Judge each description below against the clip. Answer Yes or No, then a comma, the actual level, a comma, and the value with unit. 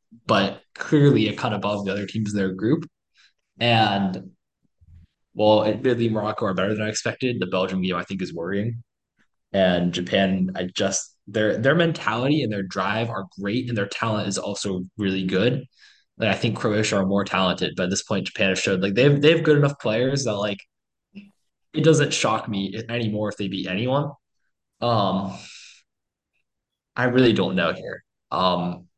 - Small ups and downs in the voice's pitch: No, average, 3.9 semitones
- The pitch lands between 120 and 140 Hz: No, low, 100 Hz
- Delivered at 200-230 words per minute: No, average, 175 wpm